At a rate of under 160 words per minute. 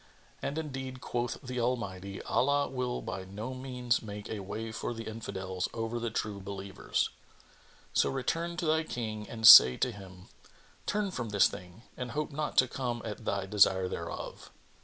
No: average, 170 wpm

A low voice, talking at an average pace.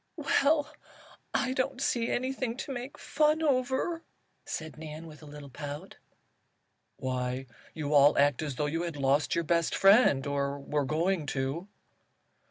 No: medium, 160 Hz; average, 150 wpm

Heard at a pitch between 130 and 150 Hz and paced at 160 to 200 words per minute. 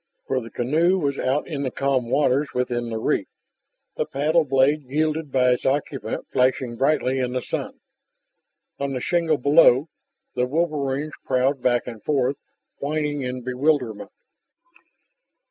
No: low, 135 Hz; average, 145 wpm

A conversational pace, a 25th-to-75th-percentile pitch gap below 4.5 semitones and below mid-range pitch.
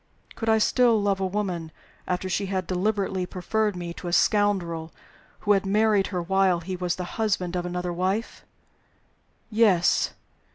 No: average, 160 wpm; narrow, 2.6 semitones; high, 190 Hz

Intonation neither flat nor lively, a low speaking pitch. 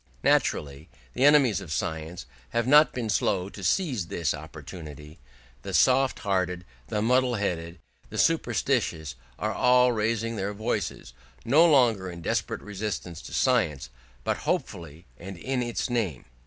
No: wide, 6.6 semitones; low, 100 Hz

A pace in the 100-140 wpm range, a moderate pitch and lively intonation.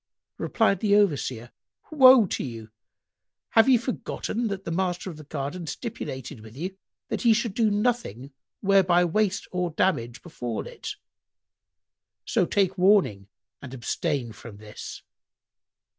Yes: slow, 135 wpm; medium, 180 Hz; wide, 8.0 semitones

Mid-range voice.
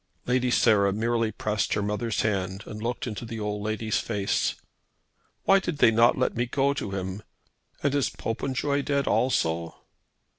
No: low, 110 Hz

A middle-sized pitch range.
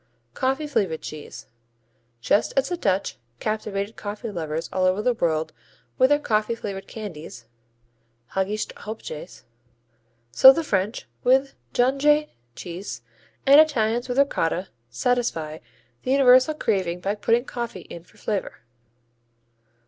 No: wide, 5.8 semitones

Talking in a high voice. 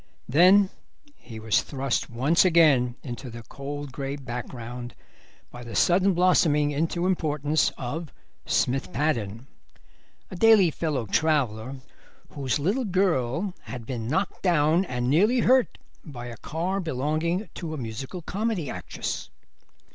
No: medium, 150 Hz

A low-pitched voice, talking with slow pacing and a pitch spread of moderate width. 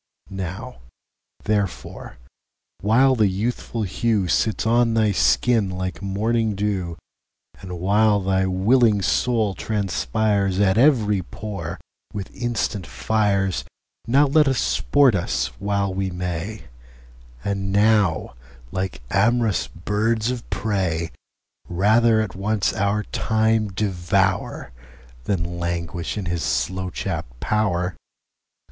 Yes: low, 100 Hz; slow, 95 wpm; average, 3.5 semitones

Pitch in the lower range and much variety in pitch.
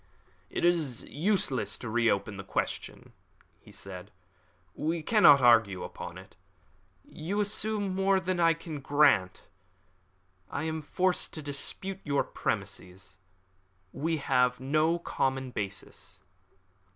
No: medium, 145 Hz; wide, 6.3 semitones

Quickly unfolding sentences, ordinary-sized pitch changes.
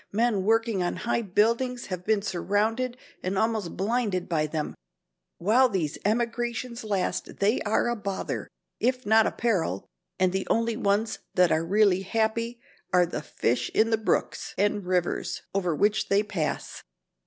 No: average, 155 wpm; average, 3.8 semitones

